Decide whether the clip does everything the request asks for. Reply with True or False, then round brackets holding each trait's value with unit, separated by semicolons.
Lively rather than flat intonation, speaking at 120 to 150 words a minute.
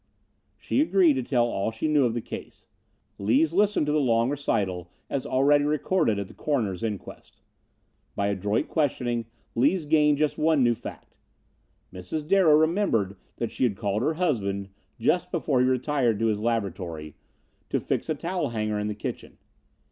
False (6.5 semitones; 170 wpm)